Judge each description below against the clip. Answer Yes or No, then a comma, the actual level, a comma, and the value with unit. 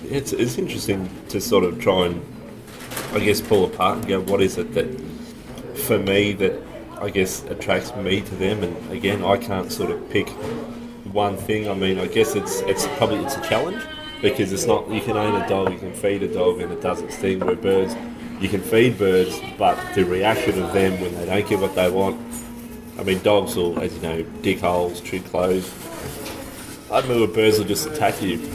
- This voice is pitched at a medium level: No, very low, 95 Hz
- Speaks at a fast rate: Yes, fast, 210 wpm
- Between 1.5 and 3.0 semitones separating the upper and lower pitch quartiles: Yes, average, 2.7 semitones